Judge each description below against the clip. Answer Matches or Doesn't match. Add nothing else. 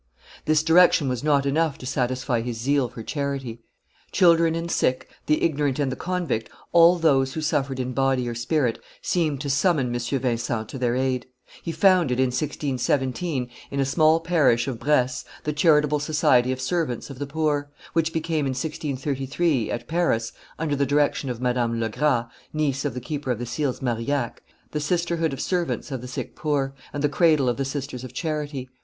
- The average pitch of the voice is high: Doesn't match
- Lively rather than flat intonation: Doesn't match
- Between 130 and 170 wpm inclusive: Doesn't match